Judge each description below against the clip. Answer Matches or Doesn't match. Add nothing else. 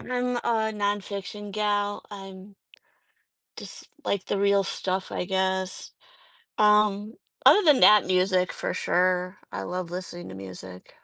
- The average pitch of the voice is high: Matches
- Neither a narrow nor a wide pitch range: Doesn't match